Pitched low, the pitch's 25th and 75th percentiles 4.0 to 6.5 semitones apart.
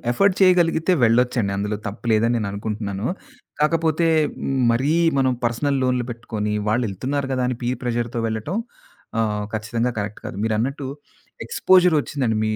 Yes: low, 120 Hz; average, 4.5 semitones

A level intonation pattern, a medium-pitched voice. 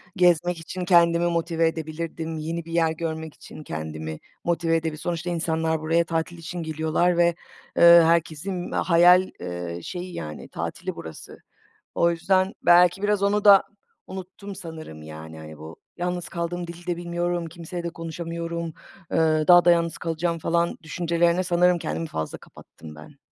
Yes: narrow, 1.7 semitones; medium, 170 Hz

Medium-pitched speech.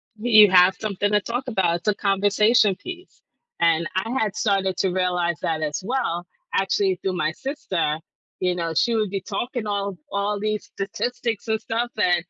No: high, 200 Hz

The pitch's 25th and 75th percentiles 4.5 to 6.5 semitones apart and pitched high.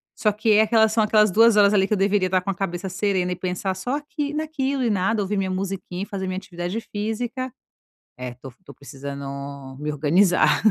No: average, 3.5 semitones; high, 195 Hz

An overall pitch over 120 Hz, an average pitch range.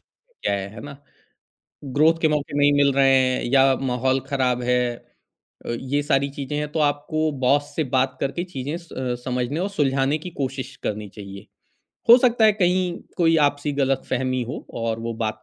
Yes: medium, 140 Hz; average, 3.3 semitones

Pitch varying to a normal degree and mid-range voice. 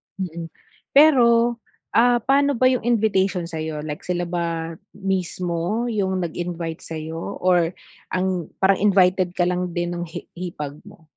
Yes: average, 3.8 semitones; medium, 180 Hz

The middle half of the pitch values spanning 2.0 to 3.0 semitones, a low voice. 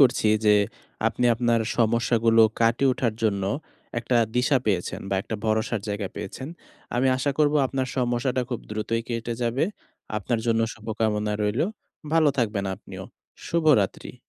Yes: average, 2.7 semitones; low, 115 Hz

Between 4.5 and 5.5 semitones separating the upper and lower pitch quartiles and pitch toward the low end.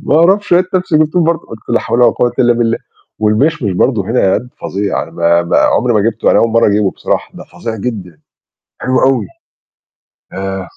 Yes: average, 5.1 semitones; low, 115 Hz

